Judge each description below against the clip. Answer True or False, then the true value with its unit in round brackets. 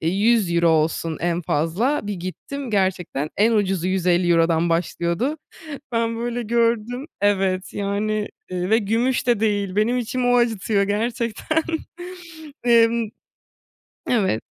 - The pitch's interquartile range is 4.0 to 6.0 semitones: True (4.6 semitones)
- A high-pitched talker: True (205 Hz)